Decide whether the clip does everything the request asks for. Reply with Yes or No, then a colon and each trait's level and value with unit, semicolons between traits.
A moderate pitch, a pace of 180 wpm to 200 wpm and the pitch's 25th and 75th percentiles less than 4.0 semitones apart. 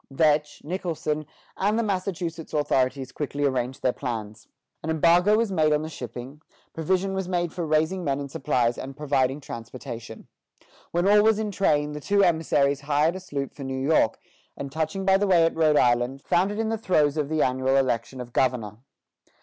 No: medium, 150 Hz; average, 190 wpm; average, 4.9 semitones